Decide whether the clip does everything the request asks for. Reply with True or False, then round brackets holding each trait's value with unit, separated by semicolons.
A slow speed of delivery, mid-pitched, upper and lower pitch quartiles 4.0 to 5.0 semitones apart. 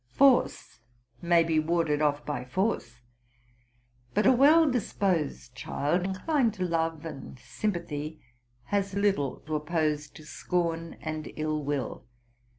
True (125 wpm; 165 Hz; 4.6 semitones)